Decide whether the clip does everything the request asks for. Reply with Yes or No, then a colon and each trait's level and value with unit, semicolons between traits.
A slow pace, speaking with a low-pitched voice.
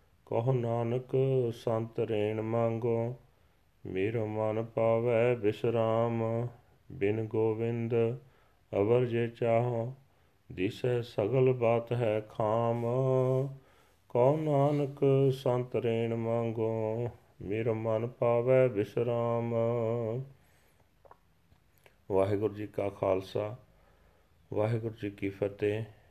Yes: slow, 75 wpm; low, 115 Hz